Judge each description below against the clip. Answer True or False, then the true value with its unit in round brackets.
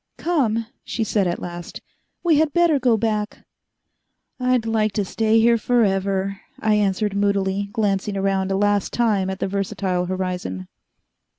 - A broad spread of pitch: False (2.8 semitones)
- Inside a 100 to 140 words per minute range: False (150 wpm)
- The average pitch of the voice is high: True (205 Hz)